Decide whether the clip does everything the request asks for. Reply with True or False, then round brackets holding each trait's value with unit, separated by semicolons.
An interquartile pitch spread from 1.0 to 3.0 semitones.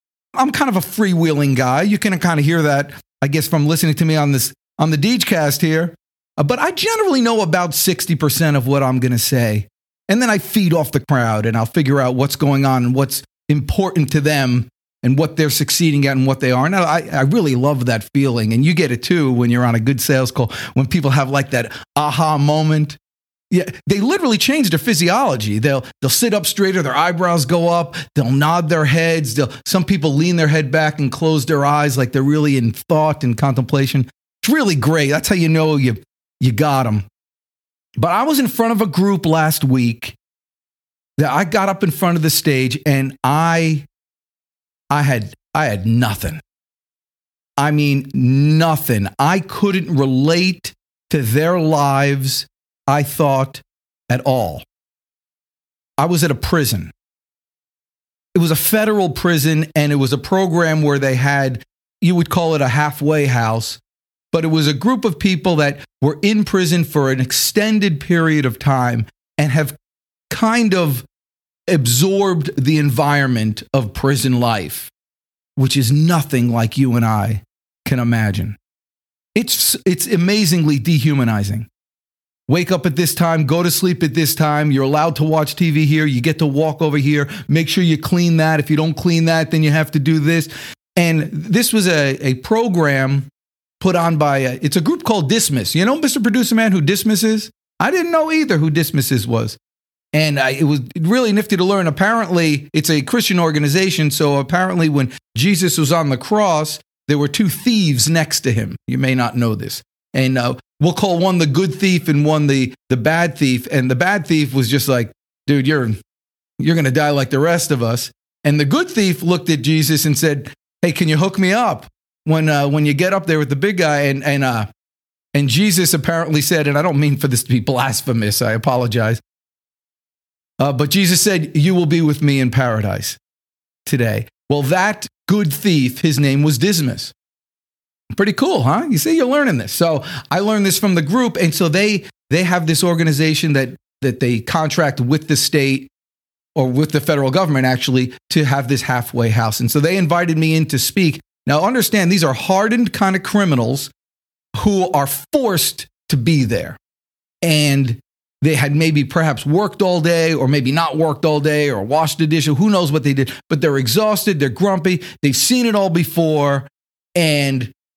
False (4.3 semitones)